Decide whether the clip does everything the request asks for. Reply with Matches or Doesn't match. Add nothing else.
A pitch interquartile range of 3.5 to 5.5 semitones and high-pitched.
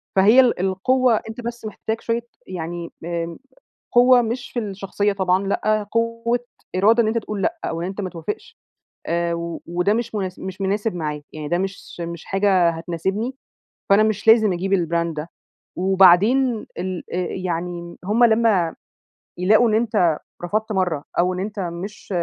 Matches